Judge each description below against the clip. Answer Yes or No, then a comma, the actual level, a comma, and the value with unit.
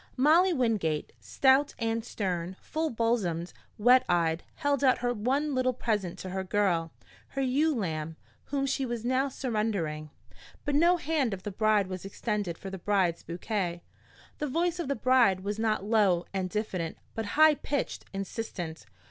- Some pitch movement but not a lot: No, wide, 6.1 semitones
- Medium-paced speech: Yes, average, 165 wpm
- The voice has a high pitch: Yes, high, 220 Hz